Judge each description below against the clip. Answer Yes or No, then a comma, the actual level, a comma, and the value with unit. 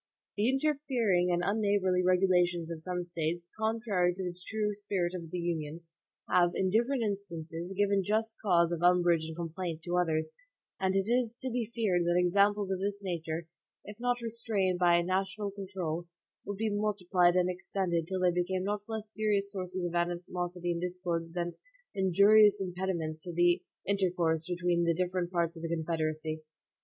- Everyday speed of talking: Yes, average, 170 wpm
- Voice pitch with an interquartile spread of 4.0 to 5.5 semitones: No, average, 2.7 semitones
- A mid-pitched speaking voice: Yes, medium, 180 Hz